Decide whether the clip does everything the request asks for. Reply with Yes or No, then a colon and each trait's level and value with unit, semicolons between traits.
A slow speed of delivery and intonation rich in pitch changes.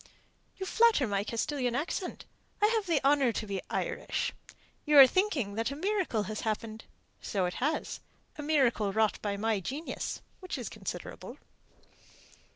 No: average, 155 wpm; wide, 6.8 semitones